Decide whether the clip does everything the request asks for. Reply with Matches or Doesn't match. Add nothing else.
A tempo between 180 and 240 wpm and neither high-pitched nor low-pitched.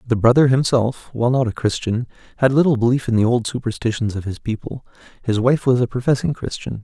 Doesn't match